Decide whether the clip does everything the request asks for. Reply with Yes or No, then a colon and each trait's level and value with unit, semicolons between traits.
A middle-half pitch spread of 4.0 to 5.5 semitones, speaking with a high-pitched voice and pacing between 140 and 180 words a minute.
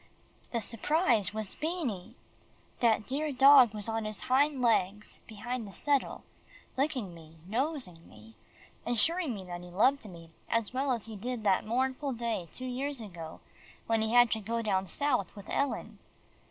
Yes: average, 4.7 semitones; high, 230 Hz; average, 165 wpm